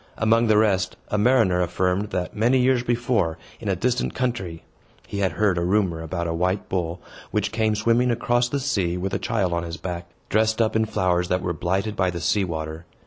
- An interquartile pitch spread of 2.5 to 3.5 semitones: No, average, 4.3 semitones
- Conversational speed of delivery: No, fast, 210 wpm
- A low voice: Yes, very low, 95 Hz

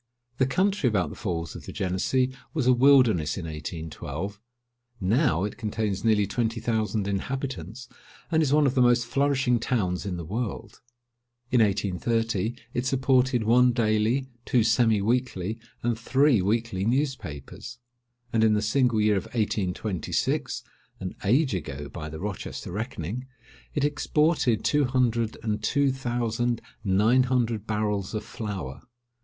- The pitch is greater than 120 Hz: No, low, 115 Hz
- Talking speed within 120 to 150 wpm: Yes, average, 145 wpm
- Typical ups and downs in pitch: Yes, average, 4.3 semitones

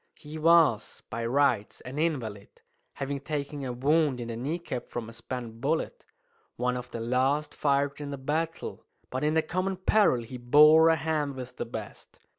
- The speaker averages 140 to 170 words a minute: No, average, 180 wpm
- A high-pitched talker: No, medium, 140 Hz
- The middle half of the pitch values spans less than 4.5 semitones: Yes, average, 4.1 semitones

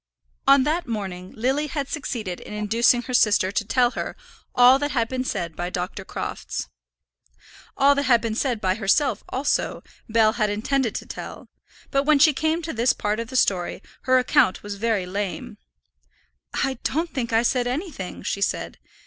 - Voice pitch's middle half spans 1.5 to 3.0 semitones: No, average, 4.8 semitones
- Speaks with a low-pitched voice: No, high, 240 Hz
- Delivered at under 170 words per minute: No, average, 180 wpm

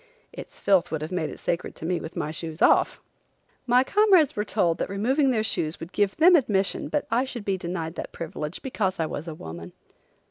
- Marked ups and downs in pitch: Yes, wide, 6.9 semitones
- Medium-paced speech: No, fast, 215 wpm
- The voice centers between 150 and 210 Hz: Yes, high, 190 Hz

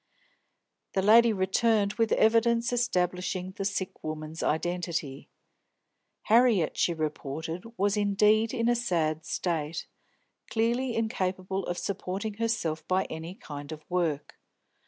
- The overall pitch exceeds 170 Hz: Yes, high, 190 Hz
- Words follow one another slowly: Yes, slow, 115 wpm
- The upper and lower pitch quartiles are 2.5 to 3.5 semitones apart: No, wide, 5.5 semitones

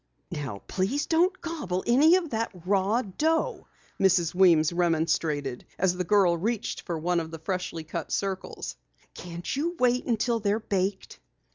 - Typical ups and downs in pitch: No, wide, 5.9 semitones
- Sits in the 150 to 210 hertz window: Yes, high, 190 Hz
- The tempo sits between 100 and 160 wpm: Yes, average, 150 wpm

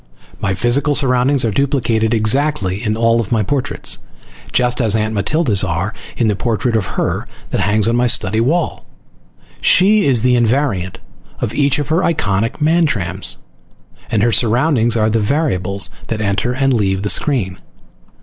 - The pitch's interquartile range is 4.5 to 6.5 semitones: Yes, average, 4.9 semitones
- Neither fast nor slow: Yes, average, 160 wpm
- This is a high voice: No, low, 115 Hz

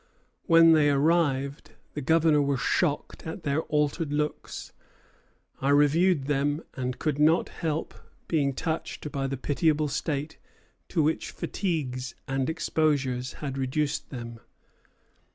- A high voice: No, medium, 145 Hz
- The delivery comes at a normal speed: No, slow, 125 wpm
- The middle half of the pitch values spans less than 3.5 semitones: Yes, average, 2.7 semitones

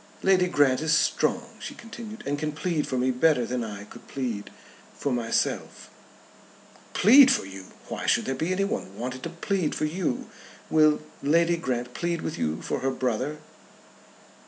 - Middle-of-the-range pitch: Yes, medium, 150 Hz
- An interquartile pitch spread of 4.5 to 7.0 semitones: Yes, wide, 5.4 semitones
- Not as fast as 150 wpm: No, average, 160 wpm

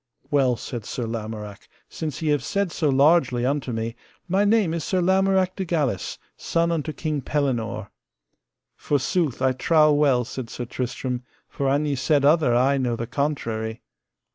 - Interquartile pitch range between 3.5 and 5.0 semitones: Yes, average, 4.6 semitones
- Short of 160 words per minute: No, average, 165 wpm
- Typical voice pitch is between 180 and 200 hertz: No, medium, 140 Hz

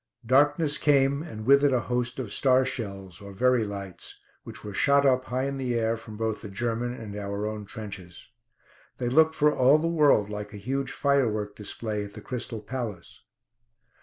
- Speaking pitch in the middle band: No, low, 120 Hz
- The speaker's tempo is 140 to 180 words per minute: No, average, 190 wpm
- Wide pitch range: No, average, 4.5 semitones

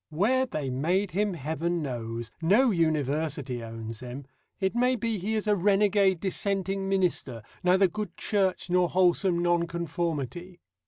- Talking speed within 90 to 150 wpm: Yes, average, 140 wpm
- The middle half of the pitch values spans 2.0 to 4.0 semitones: No, average, 4.7 semitones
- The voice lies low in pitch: No, medium, 175 Hz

